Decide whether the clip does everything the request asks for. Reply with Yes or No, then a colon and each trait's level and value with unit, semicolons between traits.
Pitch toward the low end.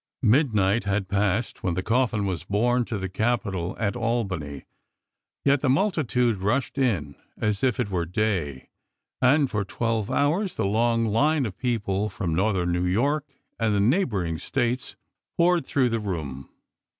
Yes: low, 110 Hz